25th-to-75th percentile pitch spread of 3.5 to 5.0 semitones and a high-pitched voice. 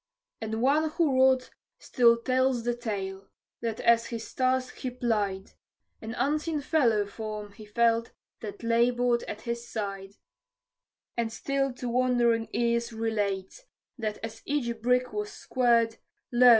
No: narrow, 2.4 semitones; high, 235 Hz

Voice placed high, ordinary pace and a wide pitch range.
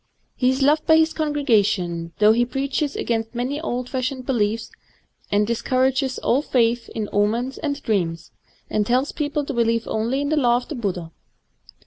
No: high, 245 Hz; average, 180 wpm; average, 4.1 semitones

